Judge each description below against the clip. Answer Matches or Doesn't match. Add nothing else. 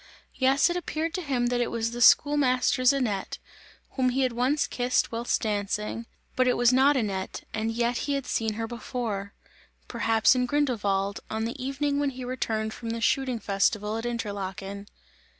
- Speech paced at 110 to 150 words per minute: Doesn't match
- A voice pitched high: Matches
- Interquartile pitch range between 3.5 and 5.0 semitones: Doesn't match